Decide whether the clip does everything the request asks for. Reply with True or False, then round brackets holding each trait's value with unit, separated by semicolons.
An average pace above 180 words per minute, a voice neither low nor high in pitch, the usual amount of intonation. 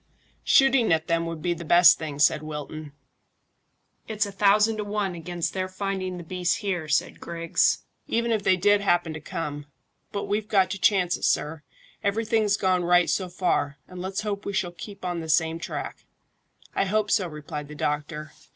True (190 wpm; 180 Hz; 3.9 semitones)